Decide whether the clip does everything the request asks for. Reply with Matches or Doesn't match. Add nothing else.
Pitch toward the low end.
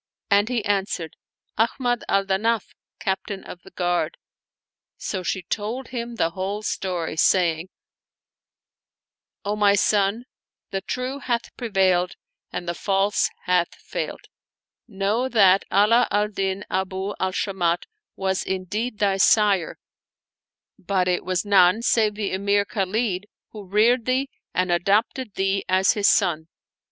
Doesn't match